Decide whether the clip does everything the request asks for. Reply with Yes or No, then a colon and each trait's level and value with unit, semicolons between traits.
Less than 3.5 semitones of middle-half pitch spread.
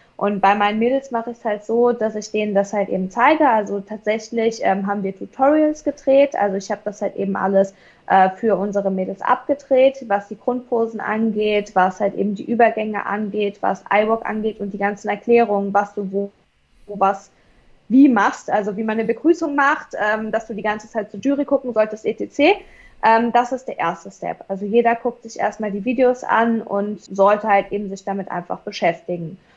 Yes: average, 2.9 semitones